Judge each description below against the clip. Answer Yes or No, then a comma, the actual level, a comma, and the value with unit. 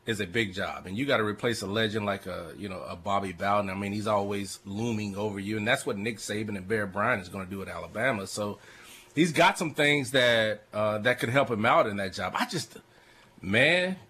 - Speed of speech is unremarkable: No, fast, 245 wpm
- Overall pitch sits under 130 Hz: Yes, low, 105 Hz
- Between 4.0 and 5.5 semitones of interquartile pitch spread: No, average, 3.1 semitones